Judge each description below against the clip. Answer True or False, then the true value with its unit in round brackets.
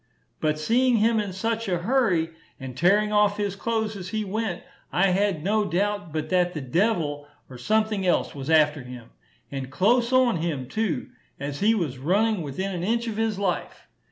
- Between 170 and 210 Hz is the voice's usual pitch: True (190 Hz)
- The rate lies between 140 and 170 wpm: False (185 wpm)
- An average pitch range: False (5.8 semitones)